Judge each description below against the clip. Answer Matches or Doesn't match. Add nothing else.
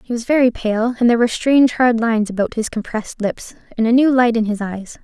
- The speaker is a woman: Matches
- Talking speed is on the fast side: Matches